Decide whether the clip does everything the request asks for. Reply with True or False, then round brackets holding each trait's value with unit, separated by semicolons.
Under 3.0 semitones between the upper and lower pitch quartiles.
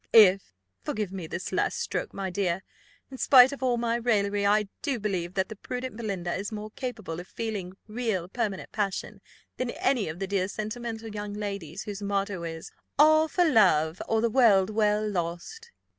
False (3.7 semitones)